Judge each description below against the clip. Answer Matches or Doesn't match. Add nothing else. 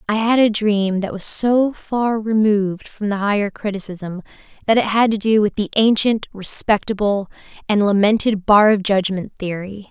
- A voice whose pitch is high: Matches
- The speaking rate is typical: Matches